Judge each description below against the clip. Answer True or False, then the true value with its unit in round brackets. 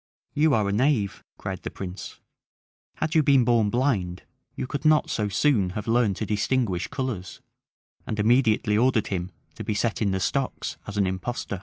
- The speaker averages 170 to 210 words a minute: True (180 wpm)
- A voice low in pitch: True (110 Hz)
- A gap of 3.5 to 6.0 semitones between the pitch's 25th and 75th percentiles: True (4.6 semitones)